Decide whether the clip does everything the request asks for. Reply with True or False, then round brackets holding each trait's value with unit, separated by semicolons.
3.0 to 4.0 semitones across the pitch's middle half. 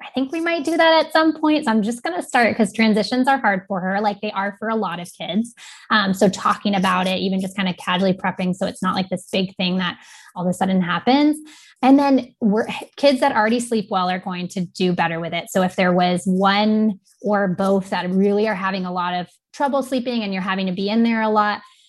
False (4.4 semitones)